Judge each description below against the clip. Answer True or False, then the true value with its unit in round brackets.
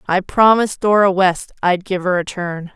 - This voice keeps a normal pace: True (195 wpm)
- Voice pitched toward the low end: False (190 Hz)